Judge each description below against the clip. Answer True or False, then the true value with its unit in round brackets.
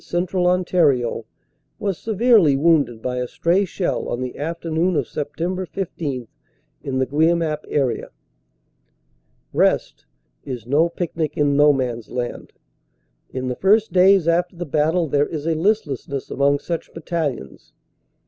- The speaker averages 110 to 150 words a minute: True (140 wpm)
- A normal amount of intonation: True (4.4 semitones)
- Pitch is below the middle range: False (155 Hz)